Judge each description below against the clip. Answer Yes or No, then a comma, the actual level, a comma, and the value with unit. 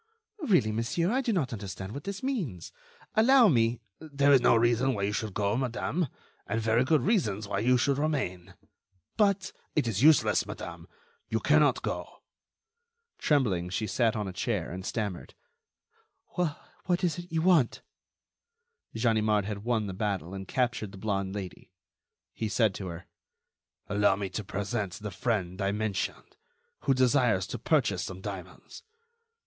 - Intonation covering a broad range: Yes, wide, 6.3 semitones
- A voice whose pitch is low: Yes, low, 110 Hz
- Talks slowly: No, average, 155 wpm